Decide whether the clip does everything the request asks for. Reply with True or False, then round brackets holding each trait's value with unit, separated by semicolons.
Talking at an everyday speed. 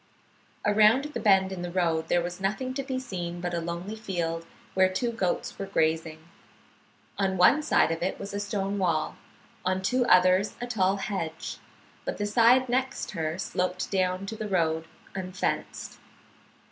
True (170 wpm)